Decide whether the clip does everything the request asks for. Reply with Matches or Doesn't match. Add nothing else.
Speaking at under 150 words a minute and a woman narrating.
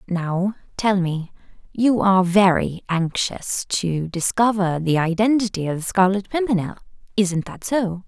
Matches